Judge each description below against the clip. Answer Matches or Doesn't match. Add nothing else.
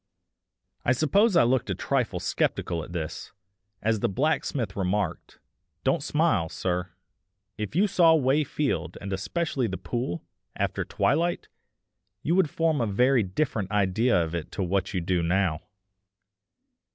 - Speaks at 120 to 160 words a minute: Matches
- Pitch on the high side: Doesn't match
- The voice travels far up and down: Matches